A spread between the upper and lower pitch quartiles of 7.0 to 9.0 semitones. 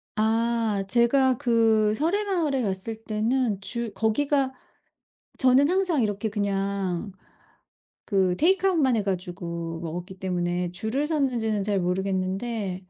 No: wide, 5.4 semitones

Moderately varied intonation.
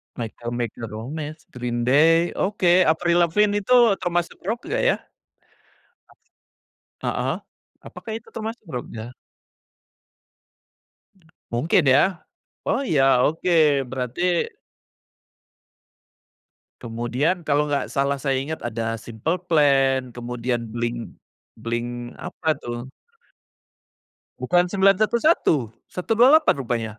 No: wide, 6.8 semitones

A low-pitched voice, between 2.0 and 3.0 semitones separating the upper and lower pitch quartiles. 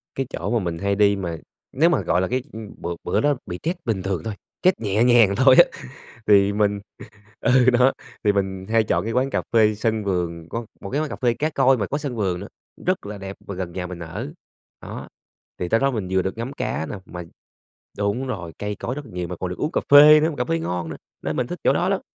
No: low, 105 Hz; wide, 5.5 semitones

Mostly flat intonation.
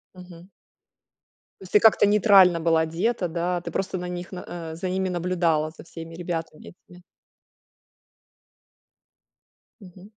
Yes: narrow, 2.0 semitones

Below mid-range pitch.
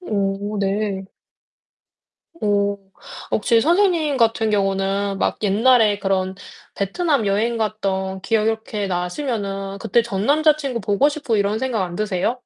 No: high, 210 Hz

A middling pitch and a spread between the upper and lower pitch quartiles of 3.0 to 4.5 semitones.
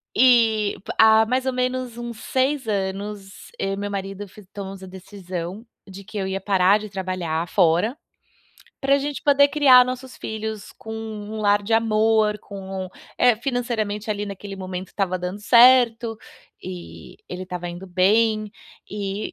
No: high, 210 Hz; average, 3.3 semitones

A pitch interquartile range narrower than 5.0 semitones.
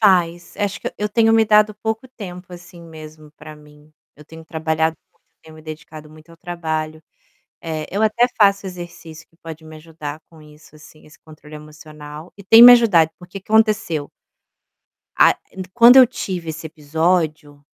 Yes: average, 4.3 semitones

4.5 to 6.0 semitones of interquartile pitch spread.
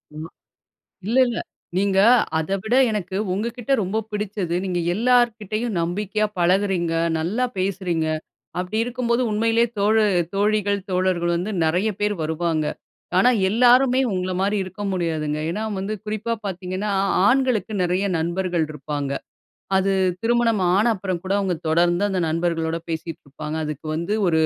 No: average, 3.9 semitones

